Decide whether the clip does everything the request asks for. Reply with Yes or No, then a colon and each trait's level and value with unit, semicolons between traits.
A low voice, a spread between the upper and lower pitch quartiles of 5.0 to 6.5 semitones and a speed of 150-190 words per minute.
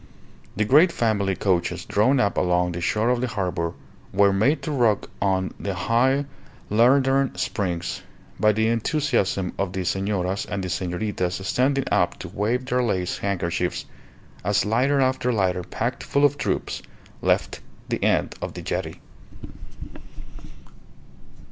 No: low, 105 Hz; average, 5.3 semitones; average, 140 wpm